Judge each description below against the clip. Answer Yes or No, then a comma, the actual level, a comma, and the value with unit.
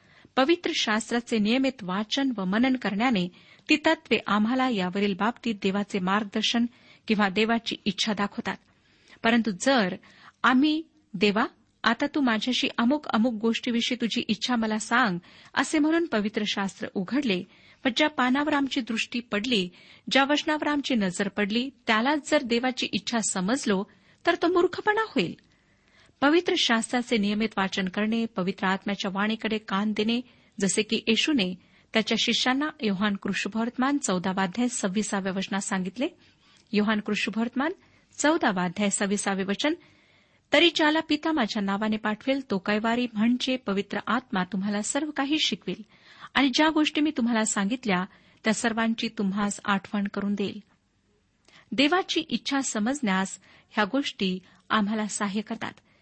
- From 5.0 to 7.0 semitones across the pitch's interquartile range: No, average, 4.4 semitones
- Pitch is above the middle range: Yes, high, 225 Hz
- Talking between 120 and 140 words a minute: Yes, average, 125 wpm